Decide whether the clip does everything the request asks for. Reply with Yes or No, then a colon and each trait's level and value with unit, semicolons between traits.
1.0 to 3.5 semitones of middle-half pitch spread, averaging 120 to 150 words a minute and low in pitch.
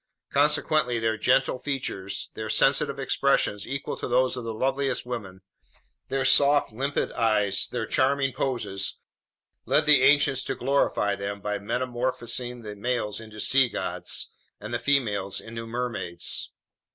No: average, 4.1 semitones; average, 140 wpm; low, 120 Hz